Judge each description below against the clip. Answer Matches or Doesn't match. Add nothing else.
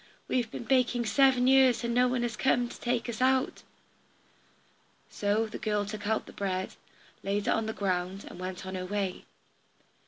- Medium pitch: Doesn't match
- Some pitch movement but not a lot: Matches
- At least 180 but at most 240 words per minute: Matches